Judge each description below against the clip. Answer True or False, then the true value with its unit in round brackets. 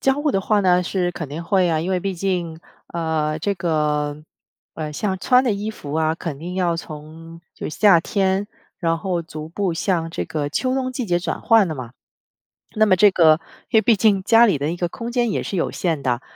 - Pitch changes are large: False (4.0 semitones)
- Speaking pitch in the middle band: True (175 Hz)